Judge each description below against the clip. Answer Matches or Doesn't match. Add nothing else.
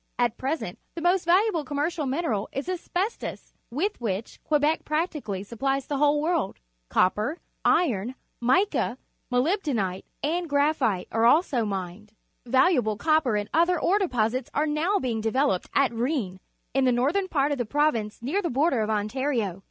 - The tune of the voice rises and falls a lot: Matches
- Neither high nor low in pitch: Doesn't match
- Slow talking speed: Doesn't match